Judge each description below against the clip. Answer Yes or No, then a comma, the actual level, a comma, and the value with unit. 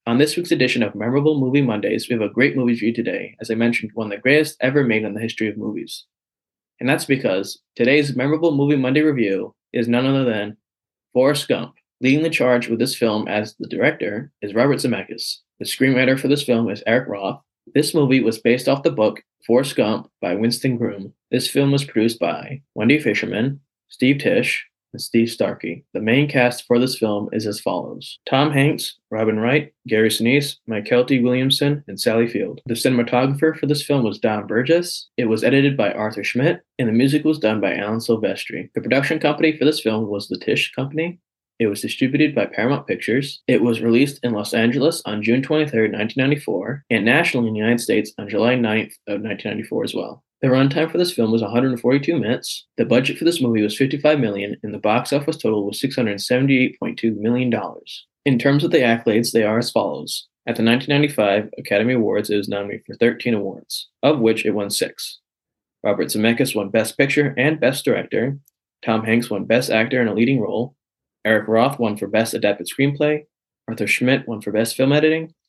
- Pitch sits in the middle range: No, low, 125 Hz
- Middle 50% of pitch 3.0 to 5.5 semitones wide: Yes, average, 4.1 semitones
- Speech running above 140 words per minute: Yes, average, 200 wpm